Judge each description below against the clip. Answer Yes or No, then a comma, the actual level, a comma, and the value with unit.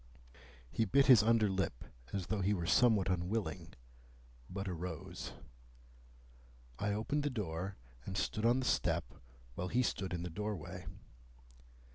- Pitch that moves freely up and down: No, average, 3.7 semitones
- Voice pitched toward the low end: Yes, low, 100 Hz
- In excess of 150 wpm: No, average, 140 wpm